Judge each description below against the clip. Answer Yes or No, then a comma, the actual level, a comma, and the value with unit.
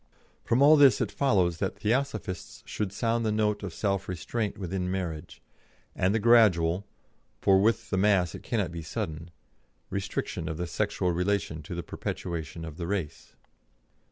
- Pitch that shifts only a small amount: No, average, 3.9 semitones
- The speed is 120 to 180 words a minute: Yes, average, 160 wpm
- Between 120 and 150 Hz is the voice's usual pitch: No, very low, 95 Hz